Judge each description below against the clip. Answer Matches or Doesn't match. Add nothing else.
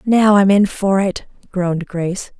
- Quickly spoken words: Doesn't match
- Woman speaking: Matches